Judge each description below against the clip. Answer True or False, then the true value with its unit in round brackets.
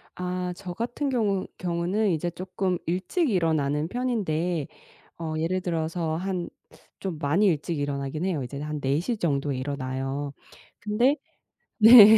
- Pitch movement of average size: True (4.7 semitones)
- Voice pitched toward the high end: False (175 Hz)